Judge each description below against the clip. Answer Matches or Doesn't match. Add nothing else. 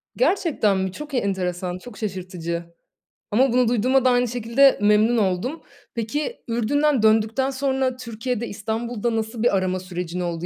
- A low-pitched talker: Doesn't match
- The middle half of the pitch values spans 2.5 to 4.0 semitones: Doesn't match